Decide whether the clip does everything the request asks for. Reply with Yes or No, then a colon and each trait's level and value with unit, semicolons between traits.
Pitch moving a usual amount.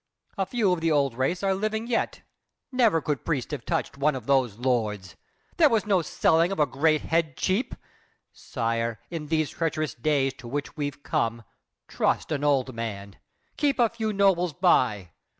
No: wide, 6.8 semitones